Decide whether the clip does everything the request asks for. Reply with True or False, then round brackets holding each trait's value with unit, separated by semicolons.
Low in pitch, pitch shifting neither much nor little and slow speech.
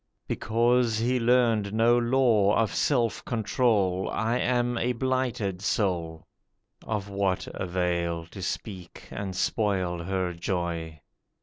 True (105 Hz; 4.5 semitones; 115 wpm)